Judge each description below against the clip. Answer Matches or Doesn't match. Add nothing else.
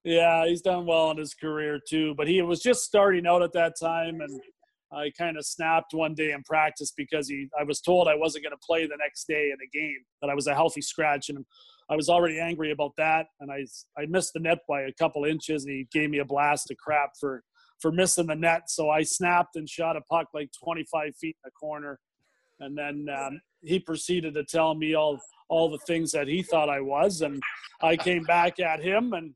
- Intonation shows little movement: Matches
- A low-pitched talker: Doesn't match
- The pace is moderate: Doesn't match